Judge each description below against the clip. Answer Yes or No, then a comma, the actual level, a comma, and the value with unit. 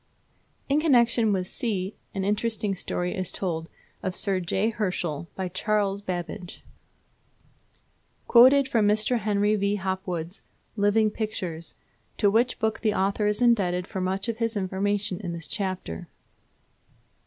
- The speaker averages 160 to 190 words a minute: No, slow, 135 wpm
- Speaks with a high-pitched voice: Yes, high, 200 Hz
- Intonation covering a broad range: No, average, 2.8 semitones